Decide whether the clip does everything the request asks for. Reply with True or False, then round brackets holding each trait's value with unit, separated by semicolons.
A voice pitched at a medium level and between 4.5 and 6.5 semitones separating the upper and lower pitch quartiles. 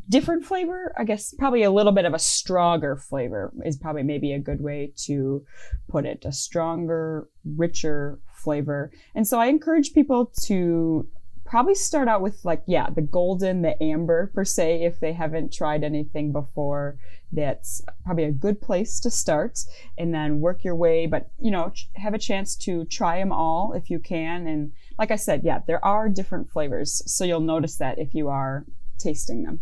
True (165 Hz; 4.9 semitones)